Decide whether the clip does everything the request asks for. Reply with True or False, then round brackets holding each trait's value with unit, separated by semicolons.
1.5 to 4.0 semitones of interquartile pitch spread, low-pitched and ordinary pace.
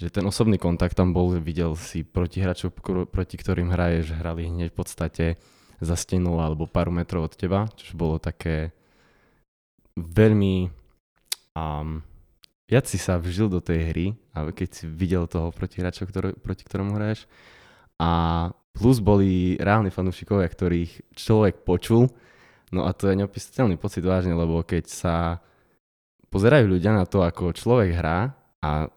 True (2.9 semitones; 90 Hz; 150 wpm)